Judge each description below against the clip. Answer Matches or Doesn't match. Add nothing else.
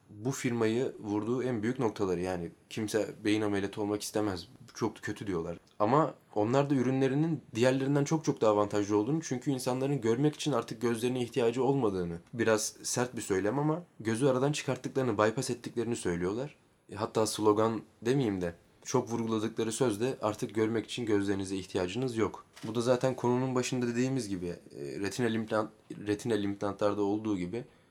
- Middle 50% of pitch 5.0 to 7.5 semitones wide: Doesn't match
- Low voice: Matches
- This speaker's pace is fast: Matches